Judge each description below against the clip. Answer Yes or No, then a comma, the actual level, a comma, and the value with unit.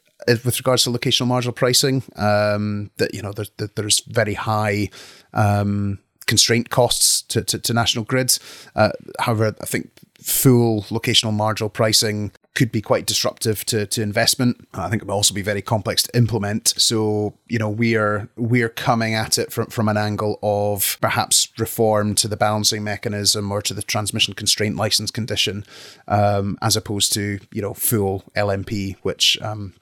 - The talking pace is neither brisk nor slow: Yes, average, 170 wpm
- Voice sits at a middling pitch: No, low, 110 Hz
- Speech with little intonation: Yes, narrow, 2.0 semitones